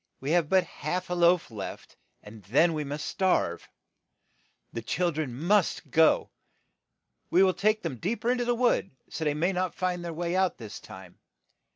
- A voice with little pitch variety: No, average, 4.2 semitones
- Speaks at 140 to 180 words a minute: No, average, 195 wpm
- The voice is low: No, medium, 170 Hz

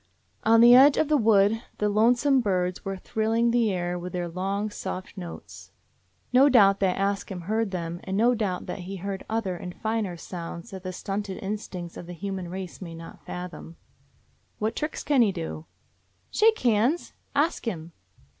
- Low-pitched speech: No, high, 195 Hz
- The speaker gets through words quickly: No, average, 180 wpm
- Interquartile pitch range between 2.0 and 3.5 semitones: No, average, 4.0 semitones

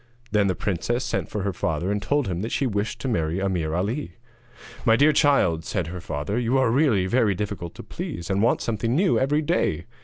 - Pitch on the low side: Yes, low, 105 Hz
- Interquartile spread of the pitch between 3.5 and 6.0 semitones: Yes, wide, 5.5 semitones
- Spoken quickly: Yes, fast, 215 wpm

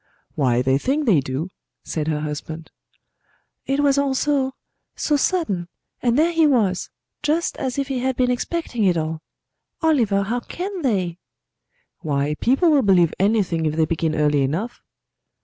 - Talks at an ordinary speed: Yes, average, 160 wpm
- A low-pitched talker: No, high, 210 Hz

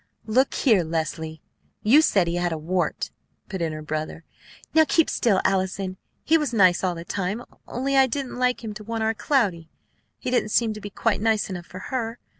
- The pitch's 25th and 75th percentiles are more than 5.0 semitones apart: Yes, wide, 5.5 semitones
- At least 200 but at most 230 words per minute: Yes, fast, 205 wpm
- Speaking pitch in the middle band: No, high, 205 Hz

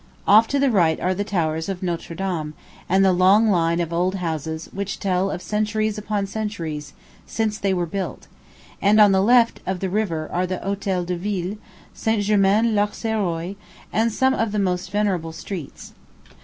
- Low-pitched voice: No, high, 195 Hz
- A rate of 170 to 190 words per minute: Yes, average, 180 wpm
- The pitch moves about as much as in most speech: Yes, average, 3.2 semitones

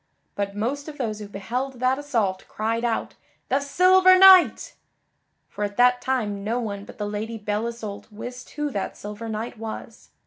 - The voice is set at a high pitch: Yes, high, 230 Hz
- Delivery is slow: No, average, 175 wpm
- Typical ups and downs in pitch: Yes, average, 4.1 semitones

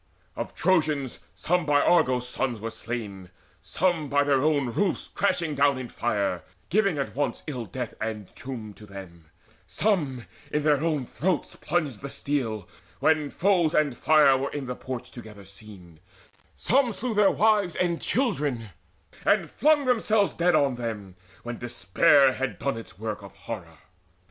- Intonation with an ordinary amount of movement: No, wide, 6.6 semitones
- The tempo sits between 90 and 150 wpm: No, average, 160 wpm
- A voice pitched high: No, low, 135 Hz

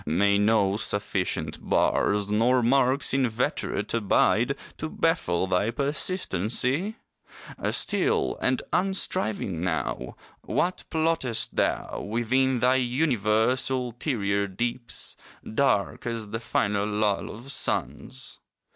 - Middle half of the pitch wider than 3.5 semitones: Yes, average, 4.4 semitones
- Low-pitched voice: Yes, low, 115 Hz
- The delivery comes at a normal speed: No, slow, 100 wpm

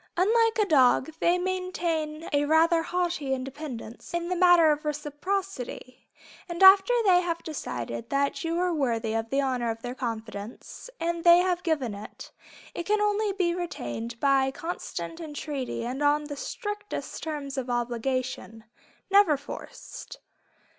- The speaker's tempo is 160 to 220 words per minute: No, average, 145 wpm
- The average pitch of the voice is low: No, very high, 305 Hz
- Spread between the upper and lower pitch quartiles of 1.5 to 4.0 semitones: No, wide, 5.6 semitones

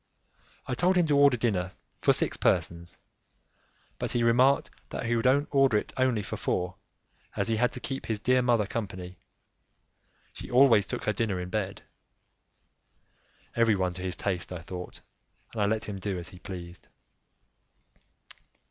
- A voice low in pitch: Yes, low, 105 Hz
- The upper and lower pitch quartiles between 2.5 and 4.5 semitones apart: No, average, 5.1 semitones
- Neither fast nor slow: Yes, average, 160 wpm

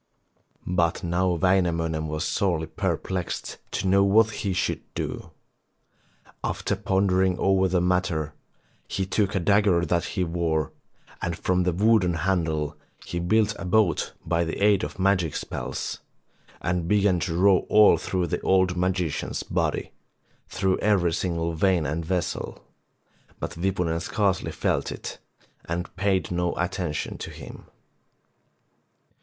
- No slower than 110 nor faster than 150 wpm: Yes, average, 140 wpm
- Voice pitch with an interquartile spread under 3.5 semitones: Yes, narrow, 2.4 semitones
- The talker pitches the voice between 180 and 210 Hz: No, very low, 90 Hz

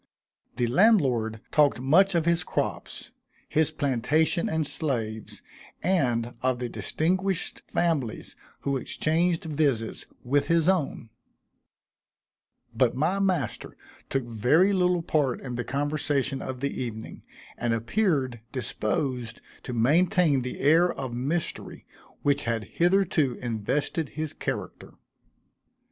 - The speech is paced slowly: Yes, slow, 115 wpm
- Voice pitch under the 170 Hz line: Yes, medium, 140 Hz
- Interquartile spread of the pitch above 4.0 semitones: Yes, average, 5.3 semitones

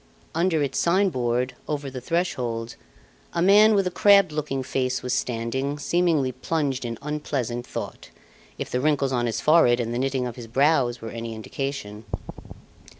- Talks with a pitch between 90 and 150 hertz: Yes, low, 135 Hz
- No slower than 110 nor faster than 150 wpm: No, average, 165 wpm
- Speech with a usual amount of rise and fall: Yes, average, 4.2 semitones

